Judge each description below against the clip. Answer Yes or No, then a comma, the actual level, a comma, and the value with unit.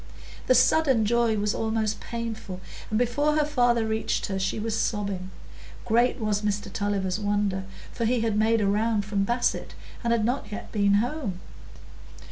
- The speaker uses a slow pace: No, average, 165 wpm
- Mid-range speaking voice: No, high, 220 Hz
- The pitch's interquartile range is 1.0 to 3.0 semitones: Yes, narrow, 2.6 semitones